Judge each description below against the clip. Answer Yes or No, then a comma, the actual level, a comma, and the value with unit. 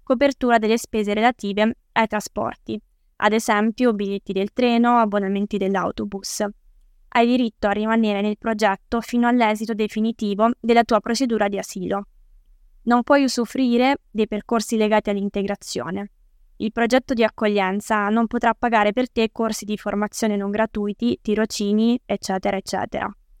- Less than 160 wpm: Yes, average, 130 wpm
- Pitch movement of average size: No, narrow, 2.3 semitones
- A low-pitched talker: No, high, 220 Hz